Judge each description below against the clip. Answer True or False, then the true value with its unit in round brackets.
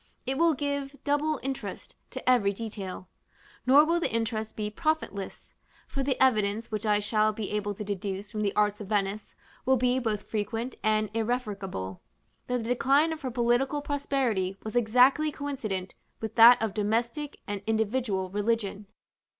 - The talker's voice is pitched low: False (225 Hz)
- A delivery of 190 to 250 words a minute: False (160 wpm)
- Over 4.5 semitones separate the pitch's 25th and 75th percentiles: False (4.2 semitones)